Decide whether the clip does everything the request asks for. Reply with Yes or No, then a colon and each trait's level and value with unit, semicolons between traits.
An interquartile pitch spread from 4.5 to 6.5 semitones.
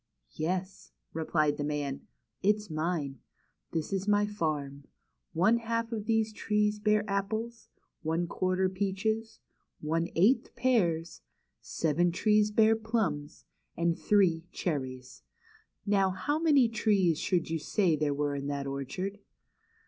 Yes: average, 5.3 semitones